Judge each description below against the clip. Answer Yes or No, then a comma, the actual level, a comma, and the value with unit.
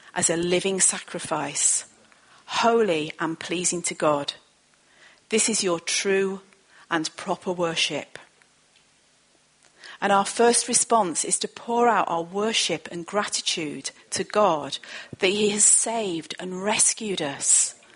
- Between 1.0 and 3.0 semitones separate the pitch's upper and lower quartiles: No, average, 3.8 semitones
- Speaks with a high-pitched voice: Yes, high, 195 Hz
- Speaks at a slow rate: Yes, slow, 125 wpm